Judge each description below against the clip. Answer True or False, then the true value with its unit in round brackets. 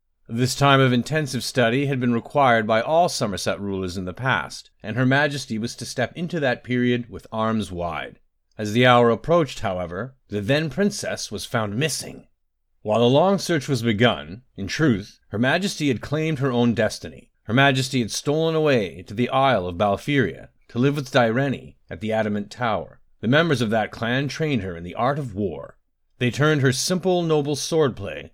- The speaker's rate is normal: True (190 wpm)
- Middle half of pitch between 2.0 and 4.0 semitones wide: False (4.7 semitones)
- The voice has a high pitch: False (125 Hz)